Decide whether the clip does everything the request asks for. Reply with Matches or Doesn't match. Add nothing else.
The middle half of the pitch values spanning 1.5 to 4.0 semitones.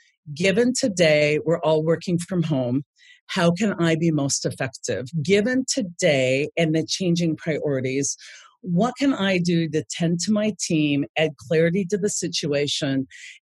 Doesn't match